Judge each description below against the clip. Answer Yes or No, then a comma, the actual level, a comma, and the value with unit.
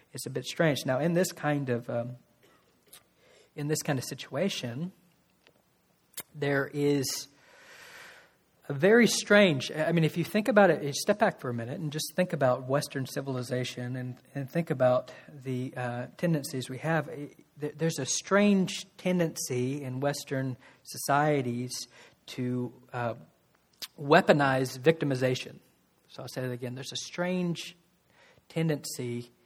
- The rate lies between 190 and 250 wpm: No, slow, 135 wpm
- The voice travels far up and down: No, average, 4.4 semitones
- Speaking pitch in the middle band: Yes, medium, 145 Hz